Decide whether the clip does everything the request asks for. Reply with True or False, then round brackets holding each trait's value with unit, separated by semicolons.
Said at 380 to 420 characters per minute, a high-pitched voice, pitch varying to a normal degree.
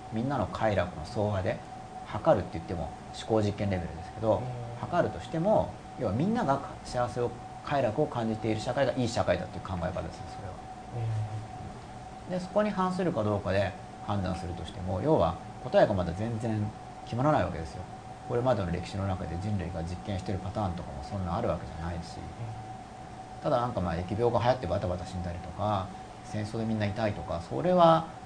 False (400 characters per minute; 105 Hz; 4.4 semitones)